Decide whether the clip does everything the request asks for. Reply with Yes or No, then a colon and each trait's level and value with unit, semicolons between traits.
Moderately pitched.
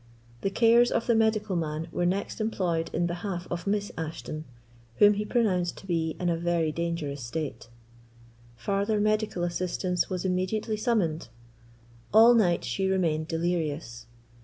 Yes: medium, 180 Hz